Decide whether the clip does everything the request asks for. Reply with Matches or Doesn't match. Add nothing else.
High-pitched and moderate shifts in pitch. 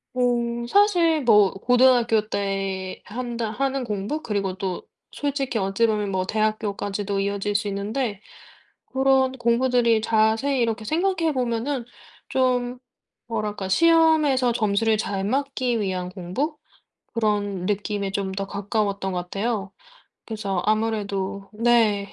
Matches